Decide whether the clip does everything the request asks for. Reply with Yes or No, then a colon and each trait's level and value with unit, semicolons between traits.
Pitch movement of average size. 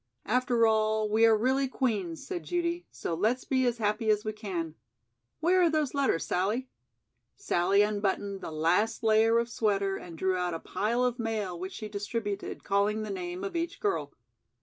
Yes: average, 3.8 semitones